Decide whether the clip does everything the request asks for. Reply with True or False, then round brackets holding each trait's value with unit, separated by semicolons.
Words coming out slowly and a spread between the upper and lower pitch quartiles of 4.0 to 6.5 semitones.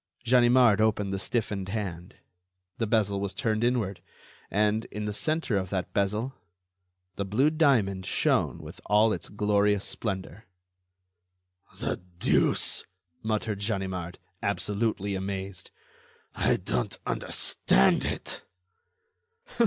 False (110 wpm; 2.4 semitones)